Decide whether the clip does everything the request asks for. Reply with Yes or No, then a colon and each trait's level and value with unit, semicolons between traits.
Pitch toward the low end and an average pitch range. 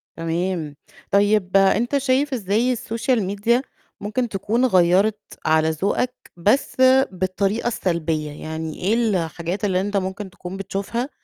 No: high, 195 Hz; average, 4.1 semitones